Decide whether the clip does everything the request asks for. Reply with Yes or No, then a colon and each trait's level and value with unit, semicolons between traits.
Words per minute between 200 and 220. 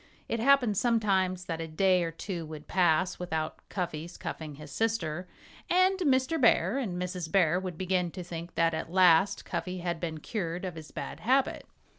No: average, 180 wpm